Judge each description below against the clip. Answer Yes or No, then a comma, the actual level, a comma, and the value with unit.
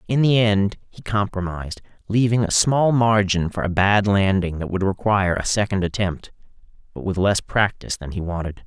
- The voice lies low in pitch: Yes, low, 100 Hz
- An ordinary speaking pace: Yes, average, 180 wpm